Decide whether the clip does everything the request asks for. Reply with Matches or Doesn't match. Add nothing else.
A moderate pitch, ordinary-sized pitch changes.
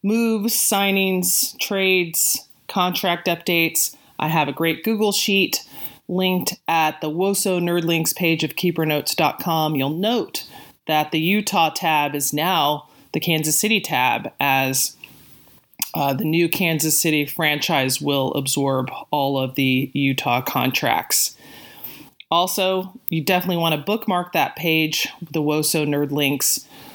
Matches